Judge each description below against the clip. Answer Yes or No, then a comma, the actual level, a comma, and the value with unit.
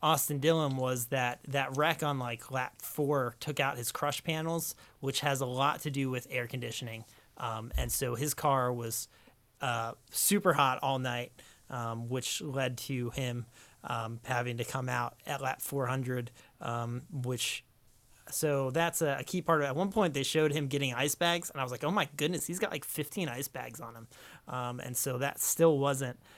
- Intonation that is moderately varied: Yes, average, 3.3 semitones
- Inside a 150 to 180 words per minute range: No, average, 200 wpm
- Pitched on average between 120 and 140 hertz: Yes, low, 135 Hz